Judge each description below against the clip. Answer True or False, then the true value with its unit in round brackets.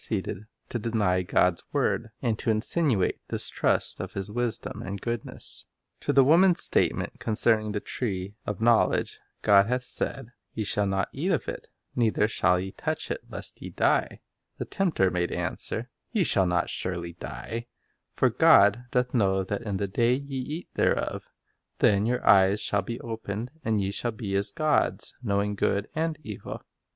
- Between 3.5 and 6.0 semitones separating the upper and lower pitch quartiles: True (3.8 semitones)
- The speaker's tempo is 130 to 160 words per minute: False (175 wpm)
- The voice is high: False (110 Hz)